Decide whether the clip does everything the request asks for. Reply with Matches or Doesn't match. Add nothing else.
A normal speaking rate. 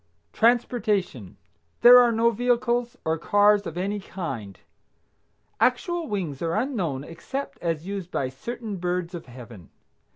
Doesn't match